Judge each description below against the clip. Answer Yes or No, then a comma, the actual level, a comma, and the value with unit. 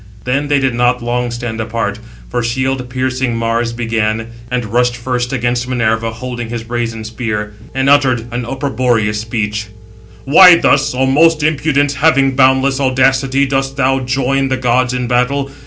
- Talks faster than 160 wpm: No, average, 155 wpm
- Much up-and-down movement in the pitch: No, narrow, 2.5 semitones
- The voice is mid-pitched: No, low, 125 Hz